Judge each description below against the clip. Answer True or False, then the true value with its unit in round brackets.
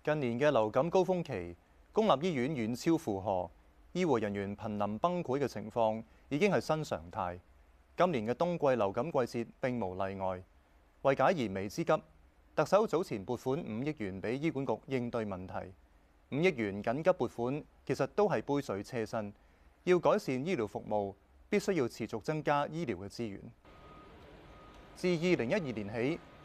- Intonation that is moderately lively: False (7.1 semitones)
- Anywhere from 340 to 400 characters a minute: False (250 characters per minute)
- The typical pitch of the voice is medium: False (115 Hz)